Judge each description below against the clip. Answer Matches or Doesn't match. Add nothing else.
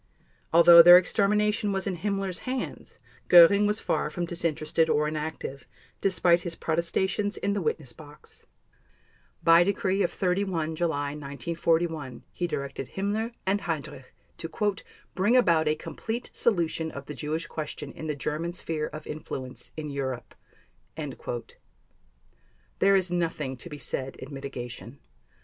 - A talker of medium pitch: Matches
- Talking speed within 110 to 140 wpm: Matches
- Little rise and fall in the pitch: Doesn't match